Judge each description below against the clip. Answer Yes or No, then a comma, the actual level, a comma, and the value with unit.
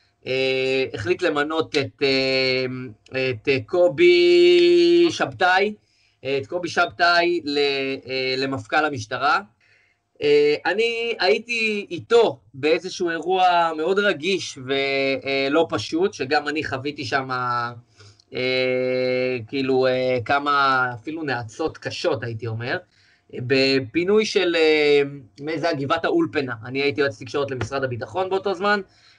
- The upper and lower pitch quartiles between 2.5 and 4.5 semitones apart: No, average, 5.2 semitones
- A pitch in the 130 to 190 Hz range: Yes, medium, 140 Hz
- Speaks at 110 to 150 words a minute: Yes, average, 115 wpm